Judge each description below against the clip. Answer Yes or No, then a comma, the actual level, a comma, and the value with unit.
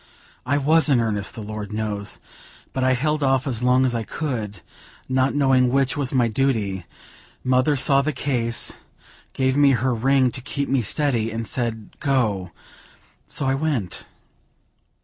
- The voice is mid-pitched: No, low, 130 Hz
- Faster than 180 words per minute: No, average, 160 wpm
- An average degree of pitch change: Yes, average, 3.4 semitones